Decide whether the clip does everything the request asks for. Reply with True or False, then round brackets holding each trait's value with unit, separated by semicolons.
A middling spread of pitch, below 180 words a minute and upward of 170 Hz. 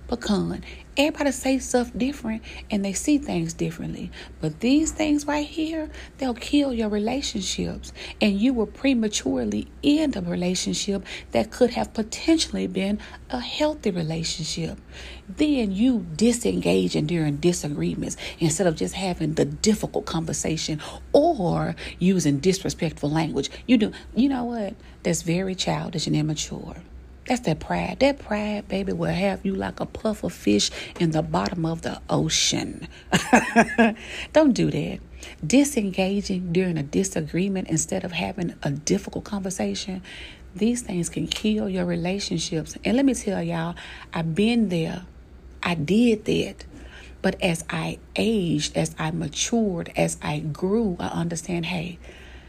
False (5.7 semitones; 145 wpm; 190 Hz)